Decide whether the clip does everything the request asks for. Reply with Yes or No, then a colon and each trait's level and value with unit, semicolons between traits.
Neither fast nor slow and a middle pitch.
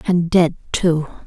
Yes: average, 145 wpm; medium, 170 Hz